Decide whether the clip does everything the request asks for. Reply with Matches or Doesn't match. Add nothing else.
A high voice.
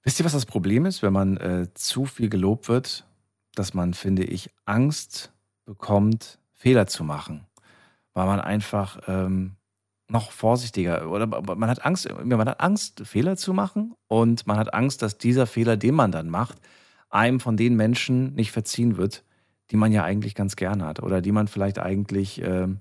Doesn't match